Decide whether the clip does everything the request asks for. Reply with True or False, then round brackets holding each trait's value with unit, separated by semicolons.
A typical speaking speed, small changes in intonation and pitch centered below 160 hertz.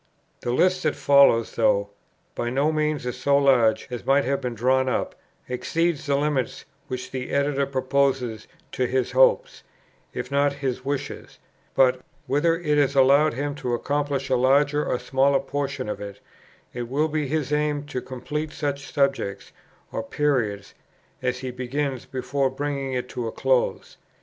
True (165 wpm; 2.3 semitones; 135 Hz)